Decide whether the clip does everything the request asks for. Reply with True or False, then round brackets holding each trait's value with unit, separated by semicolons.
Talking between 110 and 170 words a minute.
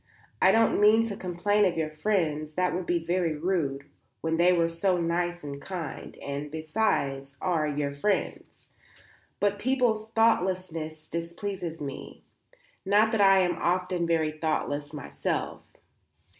True (145 wpm)